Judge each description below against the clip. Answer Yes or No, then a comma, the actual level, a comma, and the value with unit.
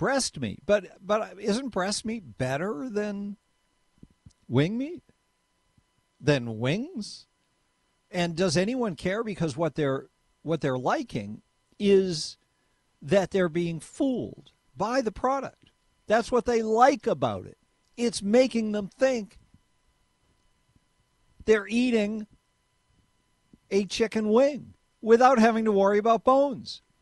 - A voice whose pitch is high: Yes, high, 210 Hz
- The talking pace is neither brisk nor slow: No, slow, 115 wpm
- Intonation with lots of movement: No, average, 4.8 semitones